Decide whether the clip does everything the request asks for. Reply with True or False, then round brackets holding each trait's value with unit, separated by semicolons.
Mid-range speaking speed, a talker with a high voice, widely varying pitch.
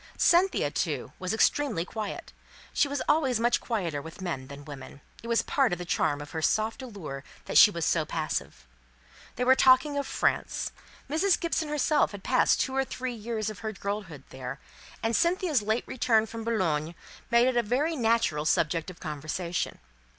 True (185 wpm; 220 Hz; 7.9 semitones)